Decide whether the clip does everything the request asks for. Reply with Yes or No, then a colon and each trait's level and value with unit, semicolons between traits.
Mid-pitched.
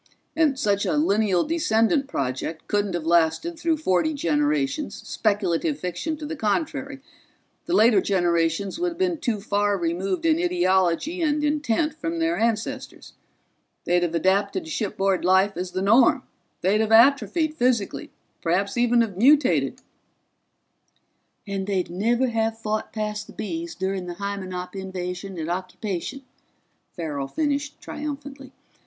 No: high, 215 Hz